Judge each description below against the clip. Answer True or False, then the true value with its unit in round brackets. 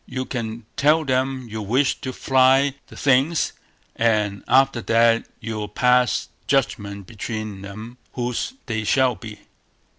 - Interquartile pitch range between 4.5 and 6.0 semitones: False (3.4 semitones)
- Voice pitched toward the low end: True (120 Hz)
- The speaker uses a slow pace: True (130 wpm)